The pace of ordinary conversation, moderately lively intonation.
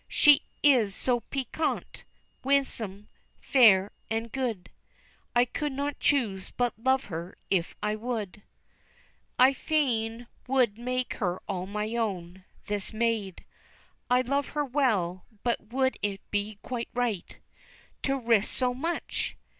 No: slow, 130 wpm; average, 4.3 semitones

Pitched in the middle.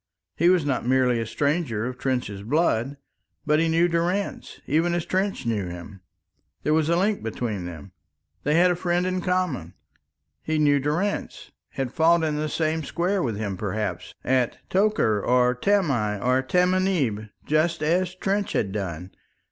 Yes: medium, 150 Hz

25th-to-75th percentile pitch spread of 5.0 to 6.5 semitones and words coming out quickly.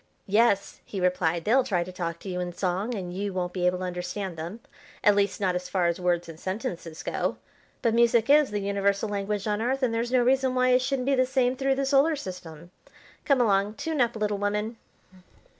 Yes: wide, 5.4 semitones; fast, 220 wpm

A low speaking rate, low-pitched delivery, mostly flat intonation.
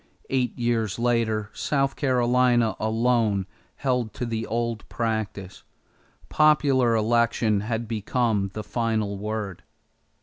Yes: slow, 105 wpm; low, 115 Hz; narrow, 2.2 semitones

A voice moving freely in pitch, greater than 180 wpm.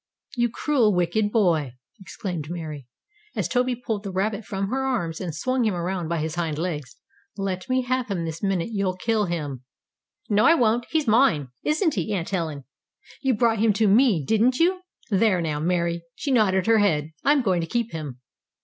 Yes: wide, 5.7 semitones; average, 190 wpm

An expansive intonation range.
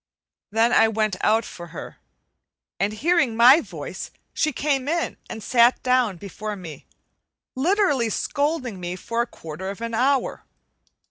No: average, 4.6 semitones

